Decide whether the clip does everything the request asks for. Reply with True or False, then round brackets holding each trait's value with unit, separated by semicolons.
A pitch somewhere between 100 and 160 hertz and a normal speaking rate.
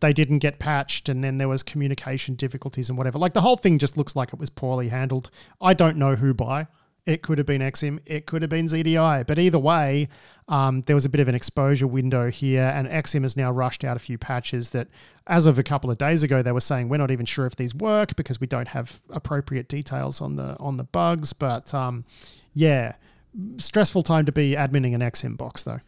False (140 Hz; 235 wpm)